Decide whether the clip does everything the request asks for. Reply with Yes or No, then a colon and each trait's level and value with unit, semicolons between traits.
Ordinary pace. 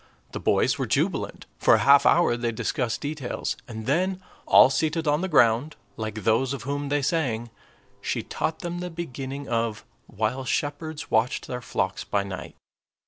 Yes: average, 170 wpm